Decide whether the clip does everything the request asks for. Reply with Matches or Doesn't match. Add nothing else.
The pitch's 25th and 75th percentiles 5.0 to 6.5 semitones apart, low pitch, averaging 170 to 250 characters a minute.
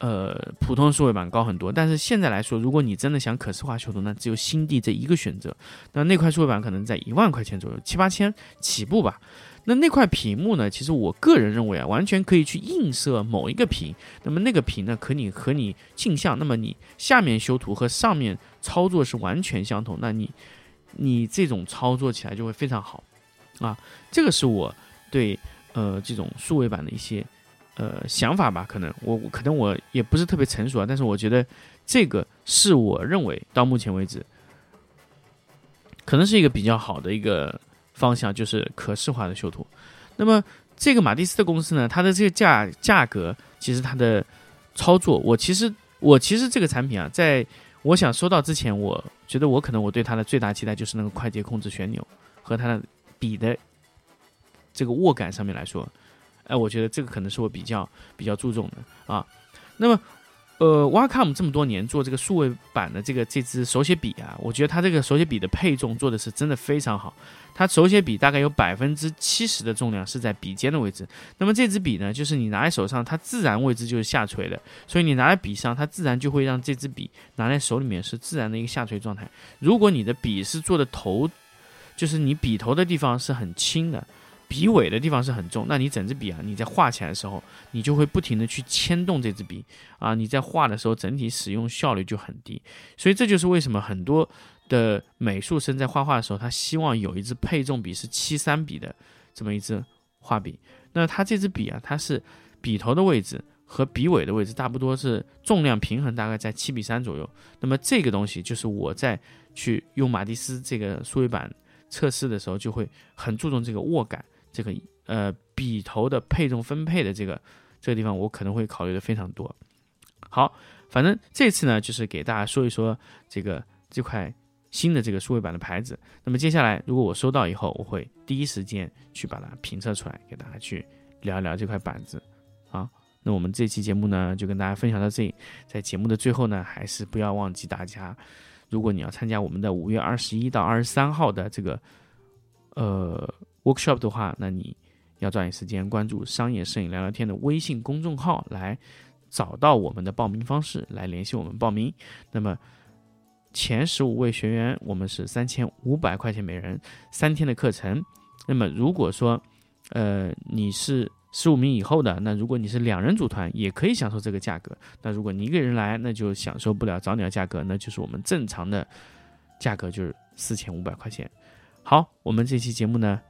Doesn't match